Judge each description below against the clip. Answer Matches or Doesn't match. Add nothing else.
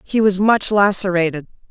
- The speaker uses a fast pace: Doesn't match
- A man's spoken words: Doesn't match